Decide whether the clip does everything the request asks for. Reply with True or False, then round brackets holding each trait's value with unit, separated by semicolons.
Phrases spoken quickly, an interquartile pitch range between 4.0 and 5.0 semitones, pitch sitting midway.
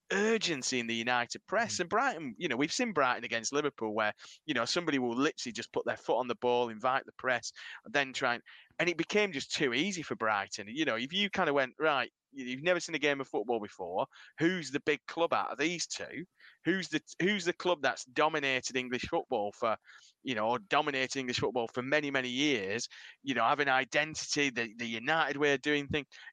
True (225 wpm; 4.3 semitones; 145 Hz)